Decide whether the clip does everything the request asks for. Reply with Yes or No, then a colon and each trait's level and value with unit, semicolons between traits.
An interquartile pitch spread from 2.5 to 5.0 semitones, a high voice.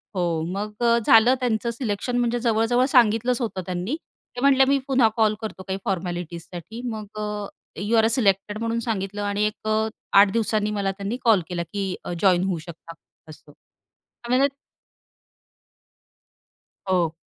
Yes: average, 3.5 semitones; high, 215 Hz